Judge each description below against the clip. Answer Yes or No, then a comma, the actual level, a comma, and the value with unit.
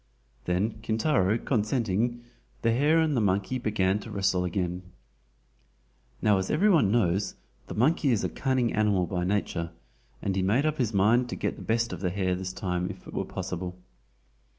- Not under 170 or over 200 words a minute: Yes, average, 180 wpm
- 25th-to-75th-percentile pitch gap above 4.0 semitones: Yes, average, 4.4 semitones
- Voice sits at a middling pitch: No, low, 105 Hz